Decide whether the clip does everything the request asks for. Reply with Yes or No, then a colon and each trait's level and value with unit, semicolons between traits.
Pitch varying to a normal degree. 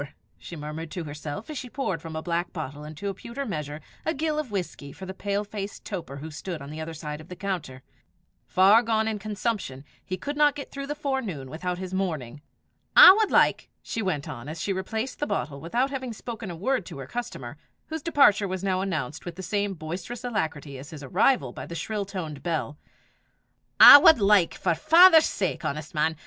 No: wide, 6.5 semitones